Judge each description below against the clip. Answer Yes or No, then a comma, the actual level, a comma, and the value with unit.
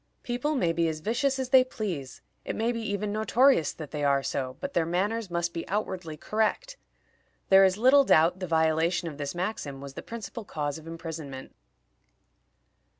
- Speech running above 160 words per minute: Yes, average, 180 wpm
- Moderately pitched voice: Yes, medium, 175 Hz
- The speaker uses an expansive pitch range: Yes, wide, 6.0 semitones